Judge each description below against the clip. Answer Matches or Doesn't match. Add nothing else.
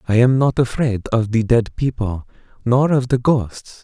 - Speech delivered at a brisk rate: Doesn't match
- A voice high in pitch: Doesn't match